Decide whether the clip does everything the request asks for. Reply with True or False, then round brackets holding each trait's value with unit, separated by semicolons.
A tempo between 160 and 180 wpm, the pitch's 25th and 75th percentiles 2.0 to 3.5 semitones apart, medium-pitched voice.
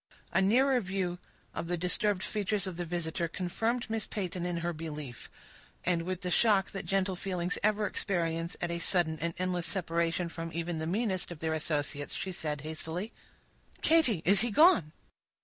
True (175 wpm; 3.0 semitones; 180 Hz)